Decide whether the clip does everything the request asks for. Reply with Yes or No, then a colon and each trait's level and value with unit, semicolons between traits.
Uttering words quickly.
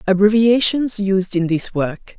No: slow, 135 wpm